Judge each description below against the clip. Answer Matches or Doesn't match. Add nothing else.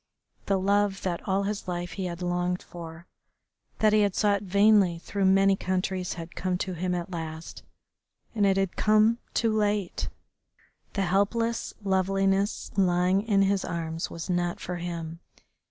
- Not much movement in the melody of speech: Matches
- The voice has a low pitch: Doesn't match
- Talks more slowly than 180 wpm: Matches